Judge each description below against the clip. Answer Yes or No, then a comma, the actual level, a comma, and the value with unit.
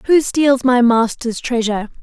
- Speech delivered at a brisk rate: No, average, 150 wpm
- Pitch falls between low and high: No, high, 245 Hz